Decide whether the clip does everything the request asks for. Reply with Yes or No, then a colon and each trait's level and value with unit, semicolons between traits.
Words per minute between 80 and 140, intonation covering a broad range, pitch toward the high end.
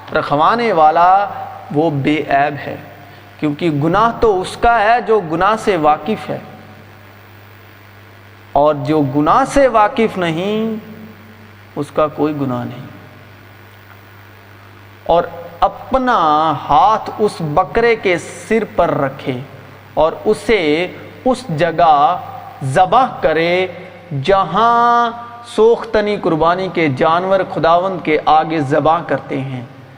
No: slow, 110 wpm; wide, 6.6 semitones; medium, 155 Hz